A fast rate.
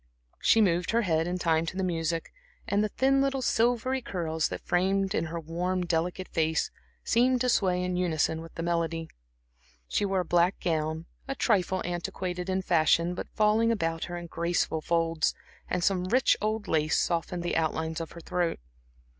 No: average, 180 wpm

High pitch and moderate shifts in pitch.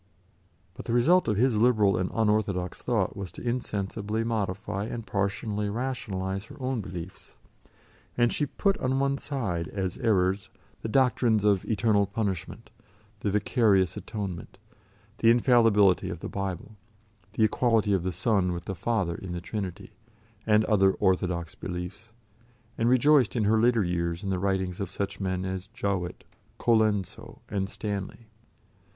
No: low, 100 Hz; average, 3.3 semitones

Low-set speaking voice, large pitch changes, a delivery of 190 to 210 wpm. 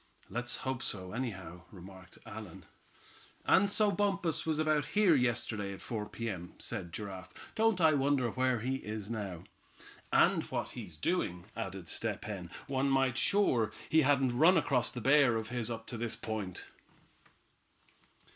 No: low, 120 Hz; wide, 5.9 semitones; average, 155 wpm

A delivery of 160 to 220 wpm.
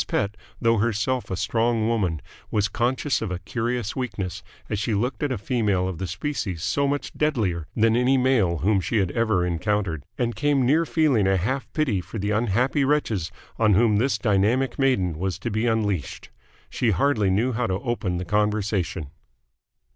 Yes: average, 180 wpm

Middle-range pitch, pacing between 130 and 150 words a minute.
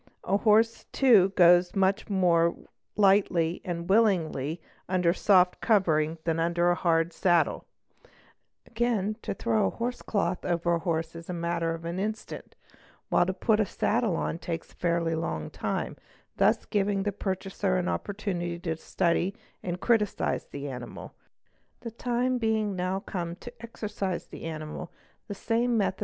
No: medium, 180 Hz; average, 160 wpm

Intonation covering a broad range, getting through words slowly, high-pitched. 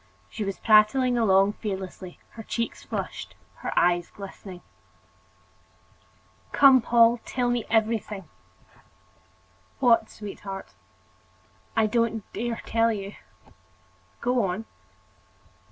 No: average, 3.0 semitones; slow, 95 wpm; high, 220 Hz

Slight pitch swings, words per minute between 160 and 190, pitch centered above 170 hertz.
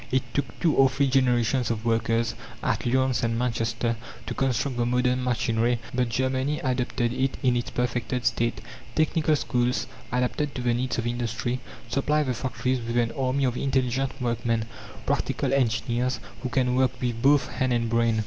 No: narrow, 1.9 semitones; average, 170 wpm; low, 125 Hz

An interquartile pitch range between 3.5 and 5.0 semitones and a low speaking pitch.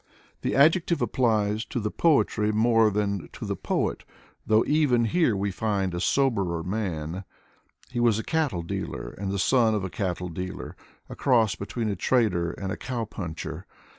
Yes: average, 4.0 semitones; low, 105 Hz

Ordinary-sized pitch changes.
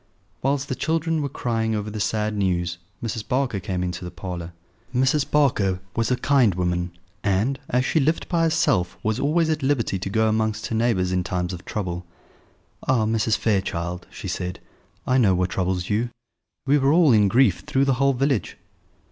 No: wide, 6.6 semitones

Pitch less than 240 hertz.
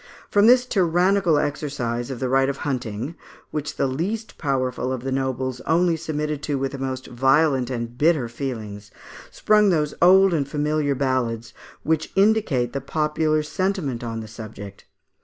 Yes: medium, 140 Hz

